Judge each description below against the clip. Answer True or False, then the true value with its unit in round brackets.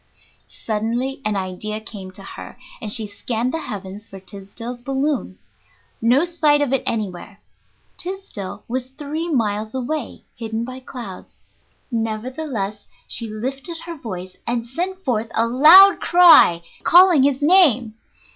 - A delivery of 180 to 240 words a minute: False (135 wpm)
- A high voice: True (240 Hz)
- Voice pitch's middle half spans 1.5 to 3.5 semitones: False (5.4 semitones)